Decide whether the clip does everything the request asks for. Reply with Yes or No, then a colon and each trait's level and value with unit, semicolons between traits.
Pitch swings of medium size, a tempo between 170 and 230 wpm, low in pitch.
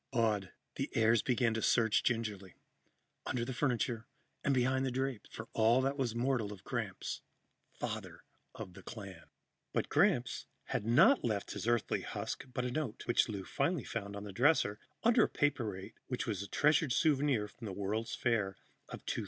Yes: average, 4.0 semitones; average, 175 wpm; low, 115 Hz